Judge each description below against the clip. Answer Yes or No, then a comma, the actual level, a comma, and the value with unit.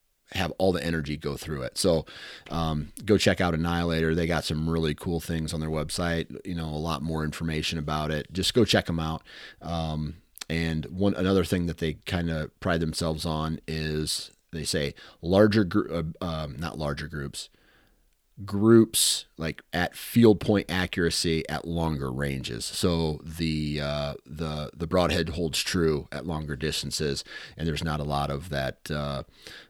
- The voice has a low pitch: Yes, very low, 80 Hz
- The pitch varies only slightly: Yes, narrow, 2.2 semitones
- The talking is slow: No, average, 170 wpm